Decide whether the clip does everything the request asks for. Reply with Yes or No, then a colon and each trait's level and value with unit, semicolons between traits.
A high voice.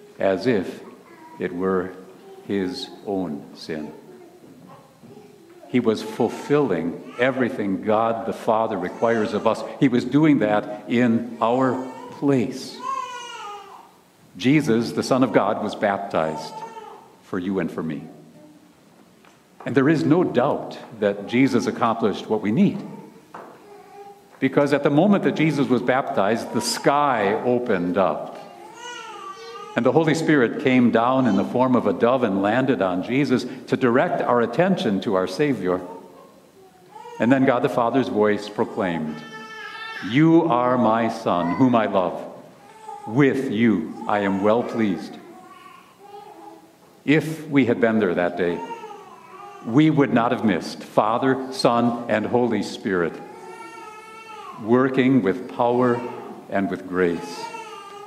No: low, 135 Hz